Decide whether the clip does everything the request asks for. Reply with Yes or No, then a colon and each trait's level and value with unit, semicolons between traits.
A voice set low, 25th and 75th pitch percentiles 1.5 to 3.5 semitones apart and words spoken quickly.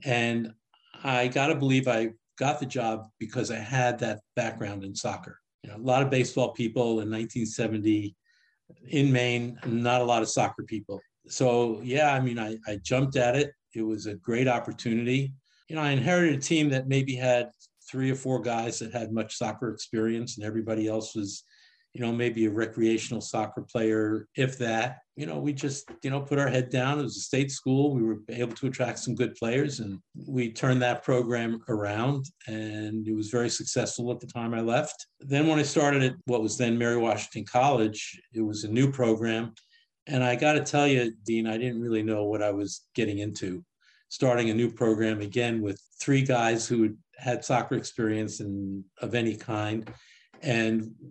No: low, 120 Hz; average, 3.0 semitones; average, 195 wpm